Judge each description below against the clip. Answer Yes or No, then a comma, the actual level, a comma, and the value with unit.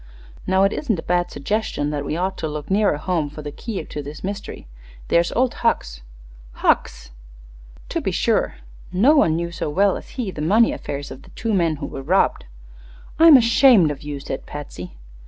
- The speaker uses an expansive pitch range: Yes, wide, 6.0 semitones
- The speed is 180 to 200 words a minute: Yes, average, 195 wpm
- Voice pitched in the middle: Yes, medium, 170 Hz